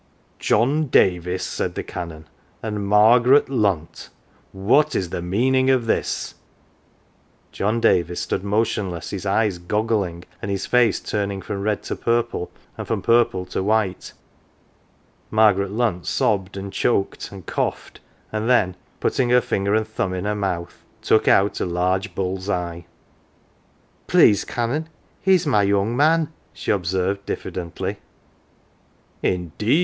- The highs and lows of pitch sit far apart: No, average, 3.8 semitones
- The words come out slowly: No, average, 145 wpm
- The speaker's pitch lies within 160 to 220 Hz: No, low, 100 Hz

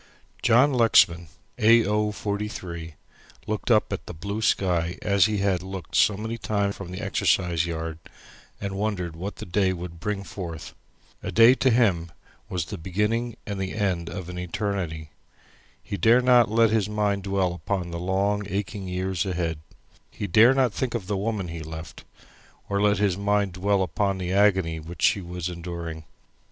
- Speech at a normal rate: Yes, average, 175 wpm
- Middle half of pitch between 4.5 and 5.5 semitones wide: No, average, 3.2 semitones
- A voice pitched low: Yes, very low, 95 Hz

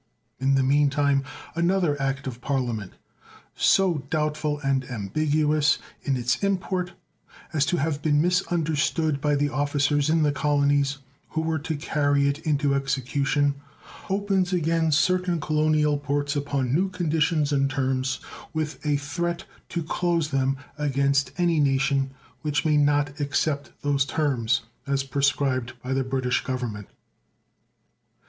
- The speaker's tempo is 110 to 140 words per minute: Yes, slow, 135 wpm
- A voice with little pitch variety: Yes, narrow, 2.3 semitones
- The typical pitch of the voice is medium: Yes, medium, 145 Hz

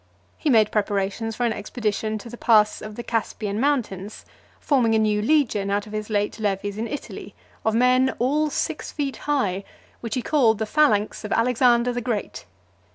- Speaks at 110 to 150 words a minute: No, average, 180 wpm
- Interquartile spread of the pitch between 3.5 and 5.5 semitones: No, average, 3.1 semitones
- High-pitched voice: Yes, high, 225 Hz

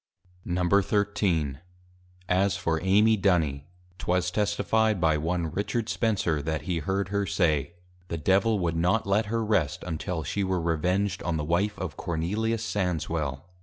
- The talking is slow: No, average, 145 wpm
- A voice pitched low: Yes, very low, 90 Hz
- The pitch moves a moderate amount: Yes, average, 3.9 semitones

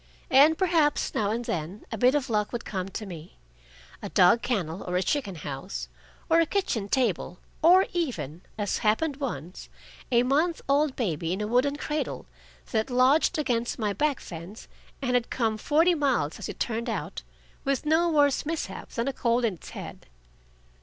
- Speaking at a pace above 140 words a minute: Yes, average, 180 wpm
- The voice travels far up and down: Yes, wide, 6.7 semitones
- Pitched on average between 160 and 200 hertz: No, high, 240 Hz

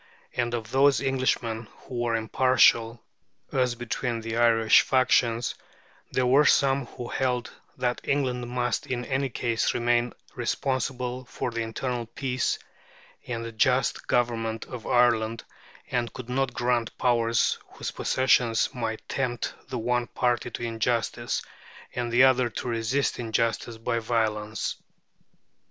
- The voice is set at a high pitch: No, low, 120 Hz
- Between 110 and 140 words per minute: Yes, slow, 135 wpm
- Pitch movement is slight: Yes, narrow, 1.7 semitones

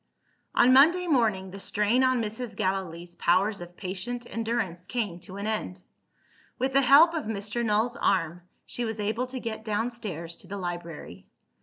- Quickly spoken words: No, average, 165 wpm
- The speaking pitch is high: Yes, high, 210 Hz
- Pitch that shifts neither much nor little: Yes, average, 4.8 semitones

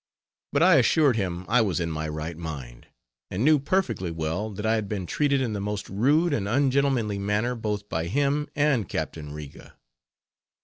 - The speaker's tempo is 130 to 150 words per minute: No, average, 185 wpm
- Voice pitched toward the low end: Yes, low, 105 Hz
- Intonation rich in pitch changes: Yes, wide, 8.0 semitones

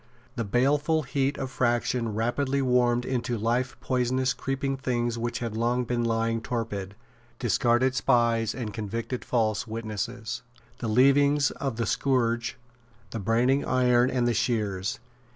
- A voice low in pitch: Yes, low, 120 Hz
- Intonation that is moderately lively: No, narrow, 2.2 semitones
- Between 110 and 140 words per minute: Yes, slow, 135 wpm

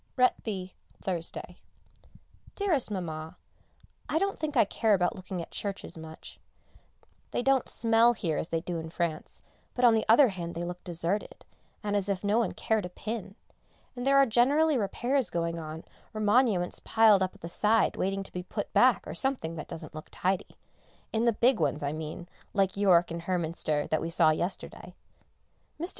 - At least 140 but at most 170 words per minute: No, average, 180 wpm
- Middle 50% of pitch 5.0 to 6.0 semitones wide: Yes, average, 5.3 semitones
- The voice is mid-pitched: No, high, 195 Hz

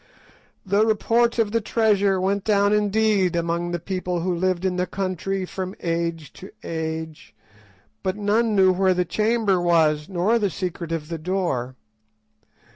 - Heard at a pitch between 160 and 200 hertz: Yes, medium, 185 Hz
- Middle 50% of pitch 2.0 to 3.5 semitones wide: Yes, average, 3.2 semitones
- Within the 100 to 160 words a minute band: Yes, average, 155 wpm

